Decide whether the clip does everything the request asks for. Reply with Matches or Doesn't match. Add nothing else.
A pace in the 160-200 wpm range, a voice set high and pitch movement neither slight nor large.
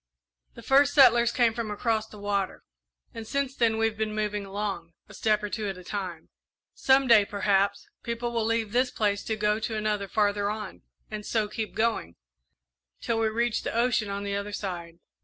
Doesn't match